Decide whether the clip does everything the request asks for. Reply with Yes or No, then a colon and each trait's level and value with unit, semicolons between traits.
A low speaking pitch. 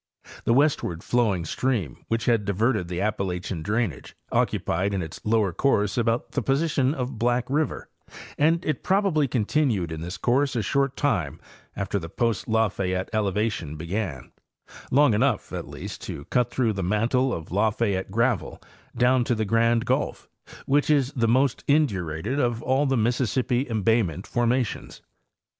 Yes: low, 115 Hz